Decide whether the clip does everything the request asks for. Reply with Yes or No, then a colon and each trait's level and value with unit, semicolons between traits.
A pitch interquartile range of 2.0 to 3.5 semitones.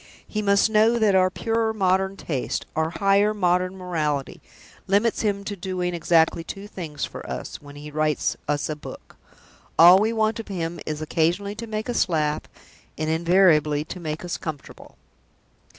No: average, 4.4 semitones